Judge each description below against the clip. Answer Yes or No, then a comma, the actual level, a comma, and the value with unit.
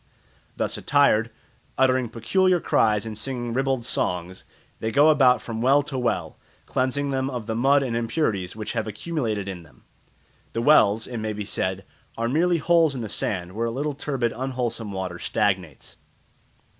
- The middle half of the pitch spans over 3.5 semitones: Yes, average, 4.3 semitones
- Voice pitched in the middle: No, low, 120 Hz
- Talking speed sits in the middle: Yes, average, 170 wpm